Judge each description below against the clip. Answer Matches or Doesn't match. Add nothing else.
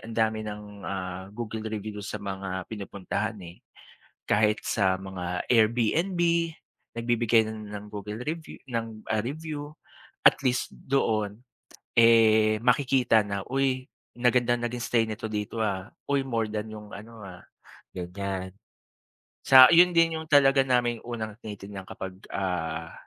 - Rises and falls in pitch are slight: Doesn't match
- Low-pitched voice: Matches